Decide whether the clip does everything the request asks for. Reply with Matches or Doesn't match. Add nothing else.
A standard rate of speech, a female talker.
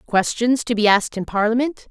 Matches